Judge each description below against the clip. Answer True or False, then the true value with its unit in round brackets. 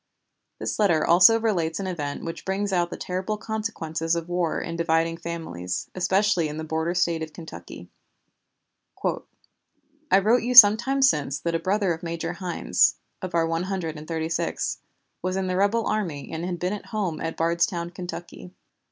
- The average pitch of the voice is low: False (175 Hz)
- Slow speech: False (180 wpm)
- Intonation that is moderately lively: True (3.1 semitones)